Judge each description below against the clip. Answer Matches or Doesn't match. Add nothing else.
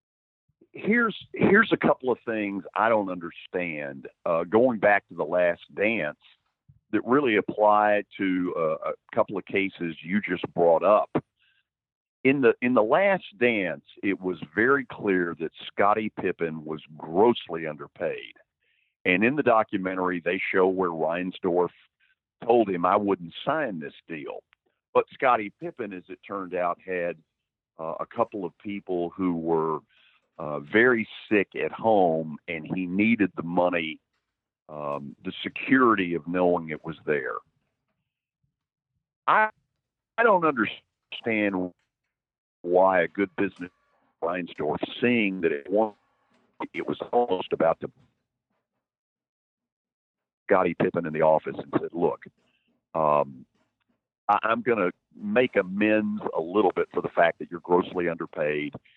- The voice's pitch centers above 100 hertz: Doesn't match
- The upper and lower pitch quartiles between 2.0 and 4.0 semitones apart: Doesn't match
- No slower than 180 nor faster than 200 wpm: Doesn't match